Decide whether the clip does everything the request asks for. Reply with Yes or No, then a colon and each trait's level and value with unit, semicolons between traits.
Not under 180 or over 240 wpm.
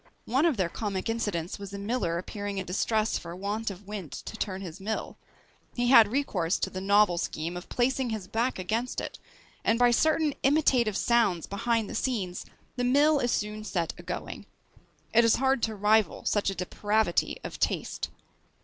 Yes: average, 185 wpm